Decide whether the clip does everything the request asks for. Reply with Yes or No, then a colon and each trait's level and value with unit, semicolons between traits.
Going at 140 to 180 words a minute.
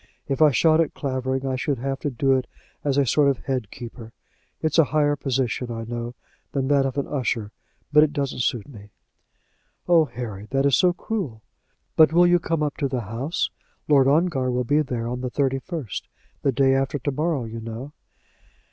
No: average, 200 wpm